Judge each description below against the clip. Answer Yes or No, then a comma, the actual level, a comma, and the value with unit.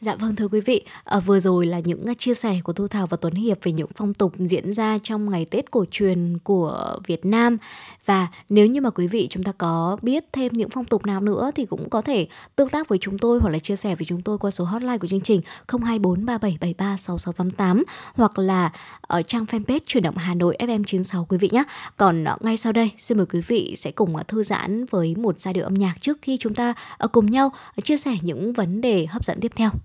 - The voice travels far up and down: No, average, 4.0 semitones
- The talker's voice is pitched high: Yes, high, 205 Hz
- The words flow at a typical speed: Yes, average, 235 wpm